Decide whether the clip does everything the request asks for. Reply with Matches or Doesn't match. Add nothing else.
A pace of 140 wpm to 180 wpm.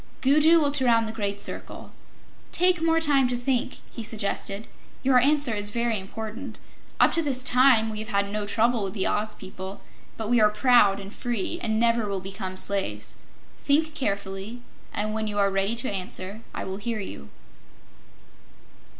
Matches